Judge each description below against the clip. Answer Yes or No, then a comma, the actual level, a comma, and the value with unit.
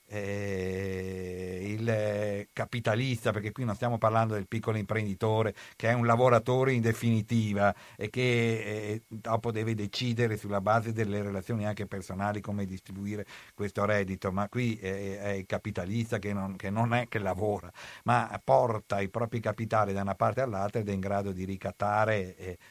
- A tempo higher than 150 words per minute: Yes, average, 165 wpm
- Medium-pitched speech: No, low, 105 Hz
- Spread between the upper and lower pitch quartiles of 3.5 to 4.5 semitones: No, narrow, 2.4 semitones